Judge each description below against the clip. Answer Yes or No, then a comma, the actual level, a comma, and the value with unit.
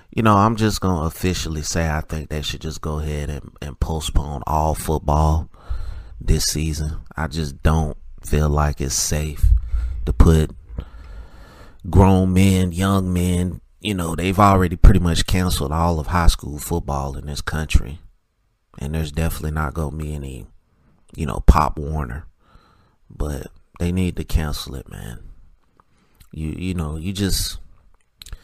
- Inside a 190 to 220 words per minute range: No, average, 150 wpm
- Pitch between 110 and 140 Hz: No, very low, 80 Hz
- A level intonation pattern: No, average, 3.0 semitones